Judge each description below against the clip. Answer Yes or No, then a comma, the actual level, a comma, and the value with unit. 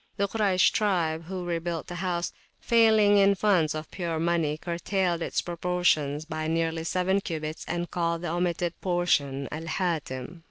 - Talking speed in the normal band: Yes, average, 155 wpm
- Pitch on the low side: No, medium, 170 Hz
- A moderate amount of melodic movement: No, narrow, 2.3 semitones